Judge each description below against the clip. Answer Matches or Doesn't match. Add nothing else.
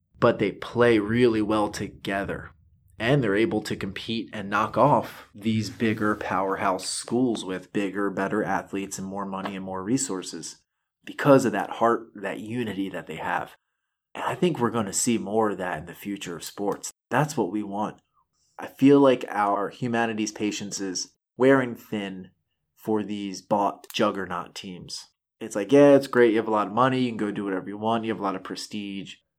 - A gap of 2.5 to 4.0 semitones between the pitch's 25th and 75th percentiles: Matches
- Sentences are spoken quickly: Doesn't match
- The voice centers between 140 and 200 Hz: Doesn't match